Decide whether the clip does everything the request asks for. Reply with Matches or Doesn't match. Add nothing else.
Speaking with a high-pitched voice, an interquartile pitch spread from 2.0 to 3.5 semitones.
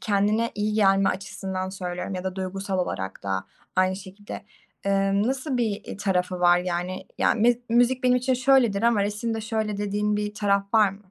Matches